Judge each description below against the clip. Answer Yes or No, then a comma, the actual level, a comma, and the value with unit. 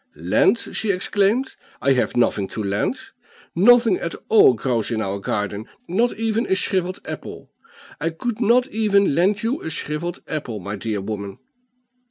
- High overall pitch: No, medium, 170 Hz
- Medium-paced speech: Yes, average, 160 wpm